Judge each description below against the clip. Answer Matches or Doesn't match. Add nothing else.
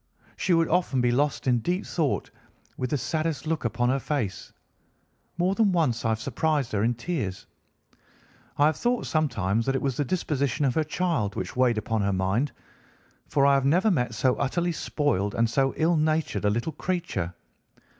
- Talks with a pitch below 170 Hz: Matches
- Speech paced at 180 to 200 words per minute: Matches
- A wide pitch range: Matches